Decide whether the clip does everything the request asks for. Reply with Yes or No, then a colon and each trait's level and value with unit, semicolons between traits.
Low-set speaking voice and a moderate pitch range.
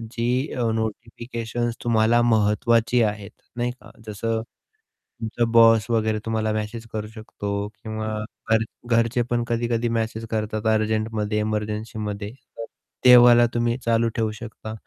No: low, 110 Hz; narrow, 1.5 semitones